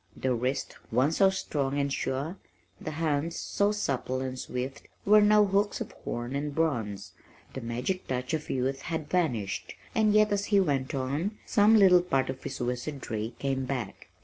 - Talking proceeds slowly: No, average, 175 wpm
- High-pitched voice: No, medium, 140 Hz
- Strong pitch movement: Yes, wide, 6.2 semitones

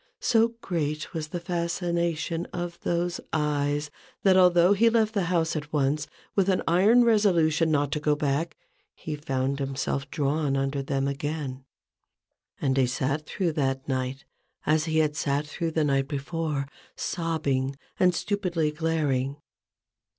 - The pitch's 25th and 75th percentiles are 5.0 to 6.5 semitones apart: No, average, 3.6 semitones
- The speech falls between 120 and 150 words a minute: Yes, average, 145 wpm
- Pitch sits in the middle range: Yes, medium, 155 Hz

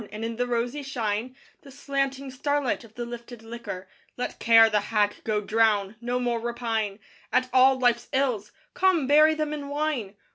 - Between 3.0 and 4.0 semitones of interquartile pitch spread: Yes, average, 3.3 semitones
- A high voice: Yes, high, 240 Hz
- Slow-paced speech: No, average, 175 wpm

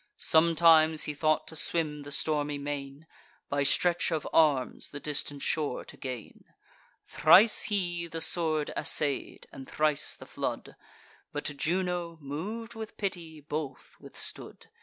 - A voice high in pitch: No, medium, 155 Hz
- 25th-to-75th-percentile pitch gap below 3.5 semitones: Yes, average, 2.7 semitones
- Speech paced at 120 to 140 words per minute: Yes, slow, 135 wpm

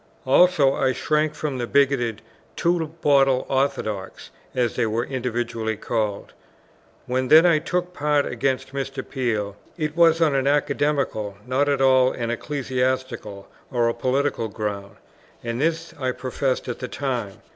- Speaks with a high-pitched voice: No, low, 130 Hz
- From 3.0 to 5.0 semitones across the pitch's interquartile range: Yes, average, 3.4 semitones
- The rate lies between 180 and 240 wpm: No, average, 145 wpm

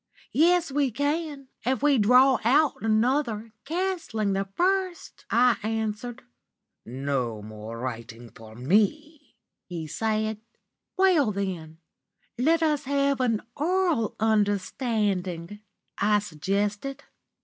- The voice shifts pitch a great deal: Yes, wide, 6.7 semitones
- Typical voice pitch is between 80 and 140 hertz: No, high, 220 Hz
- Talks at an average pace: No, slow, 105 wpm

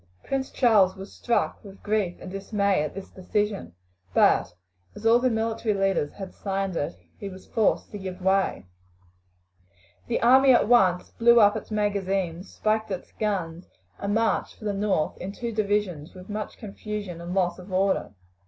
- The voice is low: No, high, 200 Hz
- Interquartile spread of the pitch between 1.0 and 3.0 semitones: Yes, narrow, 2.5 semitones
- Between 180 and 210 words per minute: No, average, 170 wpm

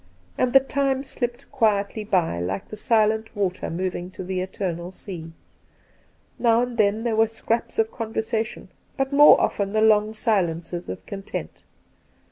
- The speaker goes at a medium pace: Yes, average, 150 wpm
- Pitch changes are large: No, average, 3.7 semitones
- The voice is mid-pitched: No, high, 215 Hz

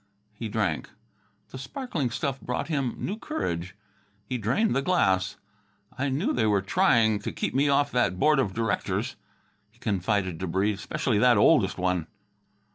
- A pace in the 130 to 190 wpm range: Yes, average, 160 wpm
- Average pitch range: No, wide, 6.1 semitones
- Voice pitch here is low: Yes, low, 115 Hz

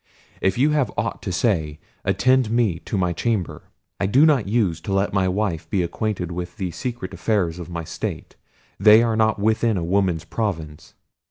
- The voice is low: Yes, low, 100 Hz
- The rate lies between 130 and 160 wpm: No, average, 185 wpm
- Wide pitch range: No, average, 4.1 semitones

